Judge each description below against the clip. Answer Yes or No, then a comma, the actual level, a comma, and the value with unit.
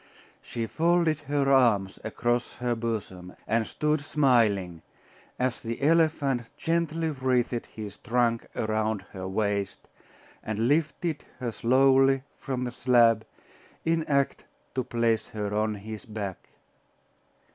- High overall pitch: No, low, 120 Hz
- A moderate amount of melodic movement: Yes, average, 4.1 semitones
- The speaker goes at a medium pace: No, slow, 120 wpm